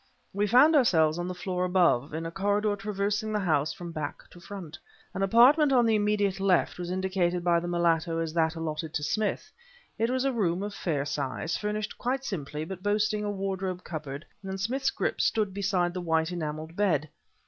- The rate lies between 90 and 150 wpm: No, average, 195 wpm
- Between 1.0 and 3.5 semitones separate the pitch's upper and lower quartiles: No, average, 4.1 semitones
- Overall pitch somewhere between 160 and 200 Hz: Yes, medium, 185 Hz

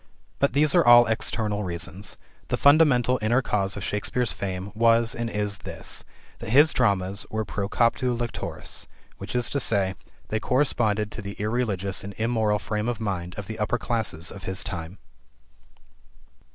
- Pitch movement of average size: Yes, average, 3.3 semitones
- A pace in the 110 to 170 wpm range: Yes, average, 150 wpm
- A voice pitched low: Yes, low, 110 Hz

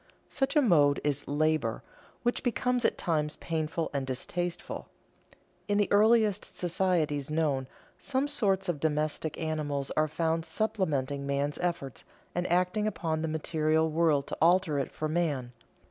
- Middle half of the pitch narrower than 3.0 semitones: No, average, 3.9 semitones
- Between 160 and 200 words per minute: No, average, 145 wpm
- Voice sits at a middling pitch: Yes, medium, 160 Hz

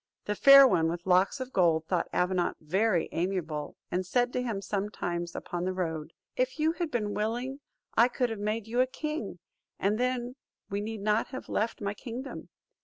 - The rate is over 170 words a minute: Yes, average, 185 wpm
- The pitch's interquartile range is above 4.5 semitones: Yes, wide, 5.5 semitones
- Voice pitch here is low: No, high, 210 Hz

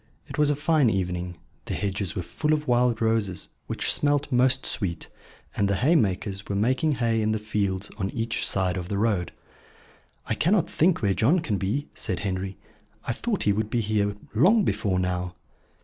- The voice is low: Yes, low, 110 Hz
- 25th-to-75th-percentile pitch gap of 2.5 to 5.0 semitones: No, wide, 5.4 semitones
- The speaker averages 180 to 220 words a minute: Yes, average, 185 wpm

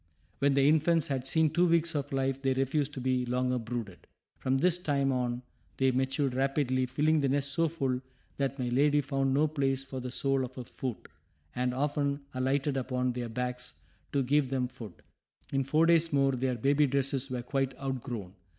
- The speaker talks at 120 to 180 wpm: No, average, 190 wpm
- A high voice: No, low, 135 Hz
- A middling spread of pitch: No, narrow, 2.0 semitones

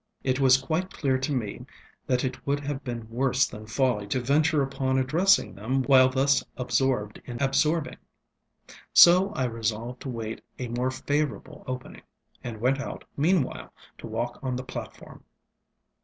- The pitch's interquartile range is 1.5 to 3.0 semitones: Yes, narrow, 2.4 semitones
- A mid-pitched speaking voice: No, low, 130 Hz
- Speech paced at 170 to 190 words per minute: No, average, 155 wpm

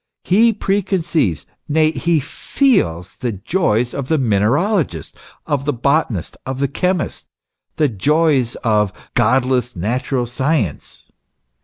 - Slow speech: Yes, slow, 120 wpm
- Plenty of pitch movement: Yes, wide, 6.0 semitones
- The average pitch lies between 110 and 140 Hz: Yes, low, 135 Hz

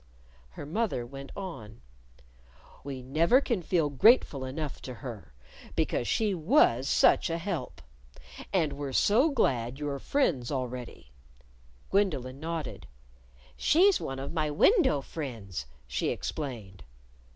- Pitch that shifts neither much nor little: No, wide, 6.2 semitones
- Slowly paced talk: Yes, slow, 120 wpm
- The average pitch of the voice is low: No, medium, 145 Hz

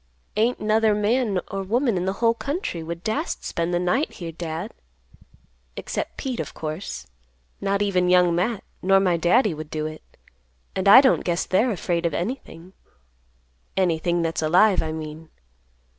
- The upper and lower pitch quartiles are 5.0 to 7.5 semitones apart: No, average, 4.6 semitones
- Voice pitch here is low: No, medium, 180 Hz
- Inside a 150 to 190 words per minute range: Yes, average, 160 wpm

